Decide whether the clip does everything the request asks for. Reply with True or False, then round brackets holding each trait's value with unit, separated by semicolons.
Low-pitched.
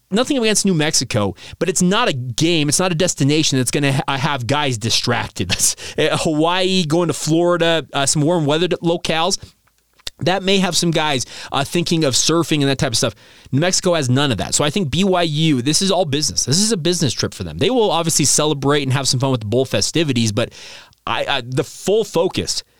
False (155 Hz)